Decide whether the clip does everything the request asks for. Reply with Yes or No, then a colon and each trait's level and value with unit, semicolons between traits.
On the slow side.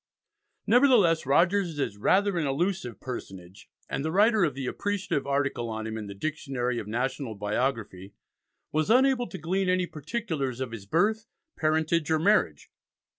No: average, 155 wpm